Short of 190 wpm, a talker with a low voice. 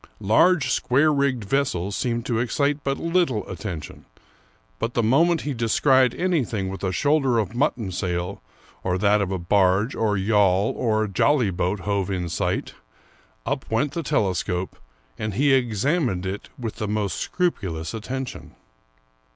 Yes: average, 155 wpm; low, 110 Hz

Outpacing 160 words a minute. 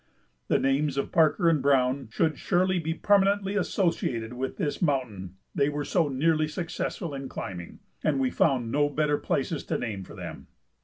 Yes: average, 170 wpm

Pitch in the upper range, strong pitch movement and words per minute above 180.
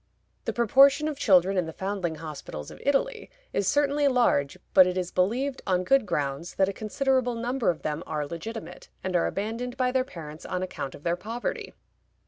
Yes: high, 195 Hz; wide, 6.8 semitones; average, 190 wpm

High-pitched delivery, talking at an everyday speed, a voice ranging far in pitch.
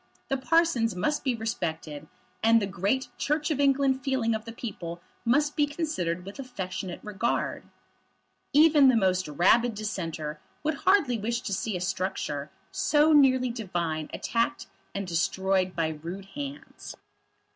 Yes: high, 225 Hz; average, 145 wpm; wide, 7.0 semitones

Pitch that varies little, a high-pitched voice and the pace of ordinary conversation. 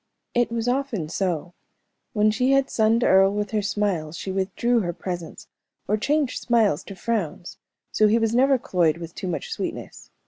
No: average, 4.6 semitones; high, 210 Hz; average, 175 wpm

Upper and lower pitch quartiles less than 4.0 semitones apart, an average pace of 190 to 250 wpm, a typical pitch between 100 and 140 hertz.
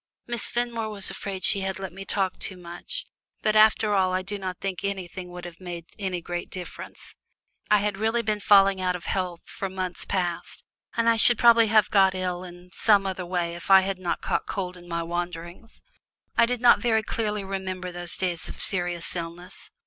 No: average, 2.8 semitones; average, 200 wpm; high, 190 Hz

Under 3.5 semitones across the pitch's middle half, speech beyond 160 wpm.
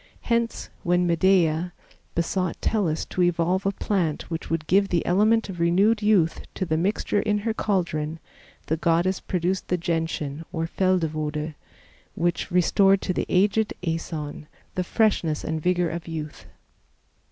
No: average, 3.0 semitones; average, 145 wpm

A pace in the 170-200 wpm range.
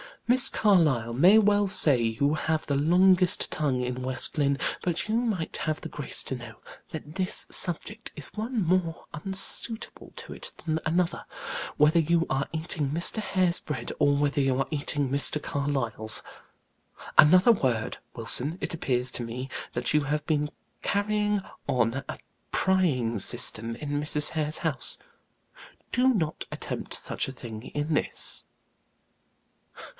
No: average, 150 wpm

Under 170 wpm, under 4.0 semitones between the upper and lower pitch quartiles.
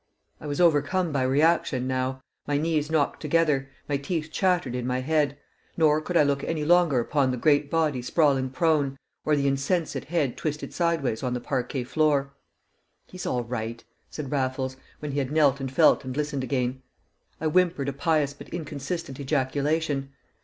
No: average, 175 wpm; average, 3.1 semitones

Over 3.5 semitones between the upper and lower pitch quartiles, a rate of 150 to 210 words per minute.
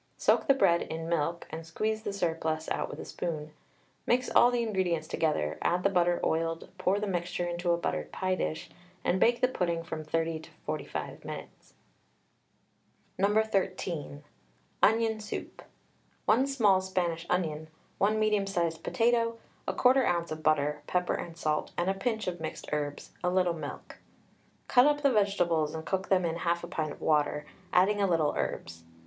Yes: average, 4.1 semitones; average, 170 wpm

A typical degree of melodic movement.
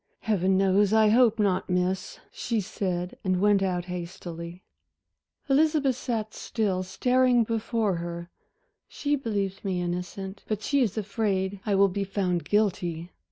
Yes: average, 3.4 semitones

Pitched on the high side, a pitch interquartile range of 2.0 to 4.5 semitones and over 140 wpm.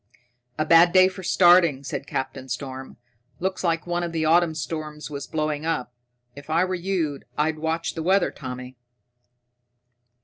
No: medium, 160 Hz; average, 3.4 semitones; average, 160 wpm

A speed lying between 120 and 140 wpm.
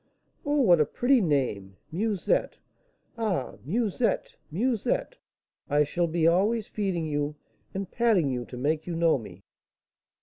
Yes: slow, 135 wpm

